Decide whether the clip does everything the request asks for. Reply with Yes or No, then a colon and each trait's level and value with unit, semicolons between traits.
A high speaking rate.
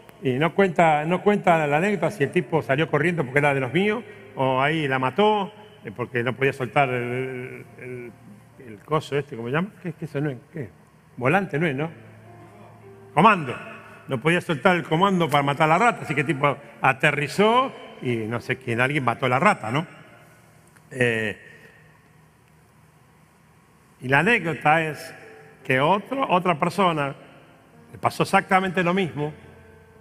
No: average, 170 wpm